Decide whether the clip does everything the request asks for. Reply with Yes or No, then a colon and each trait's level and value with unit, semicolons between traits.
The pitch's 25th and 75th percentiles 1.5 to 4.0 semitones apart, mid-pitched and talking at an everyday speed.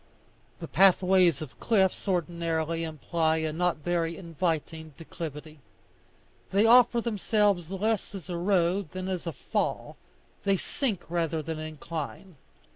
No: average, 3.1 semitones; medium, 170 Hz; slow, 125 wpm